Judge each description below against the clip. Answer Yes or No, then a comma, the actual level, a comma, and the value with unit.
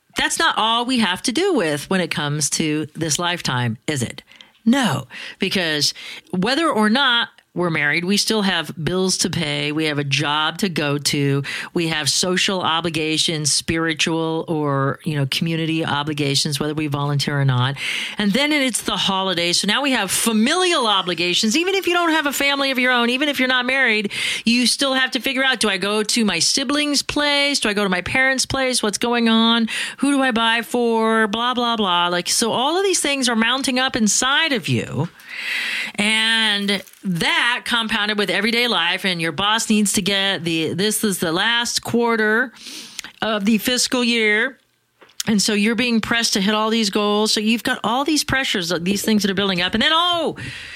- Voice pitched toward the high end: Yes, high, 215 Hz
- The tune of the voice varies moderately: No, wide, 6.4 semitones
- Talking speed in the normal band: Yes, average, 195 wpm